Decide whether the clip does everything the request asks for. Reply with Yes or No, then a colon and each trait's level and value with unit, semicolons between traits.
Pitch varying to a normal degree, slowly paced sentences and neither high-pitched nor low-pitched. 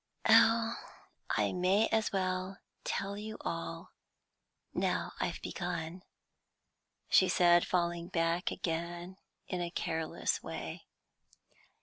No: narrow, 2.3 semitones; slow, 100 wpm; medium, 180 Hz